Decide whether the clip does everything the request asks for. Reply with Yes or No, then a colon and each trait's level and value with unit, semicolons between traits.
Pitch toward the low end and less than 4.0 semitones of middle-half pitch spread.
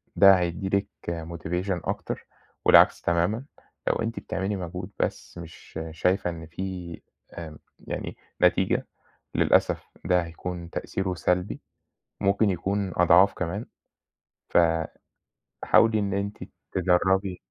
Yes: very low, 90 Hz; narrow, 2.4 semitones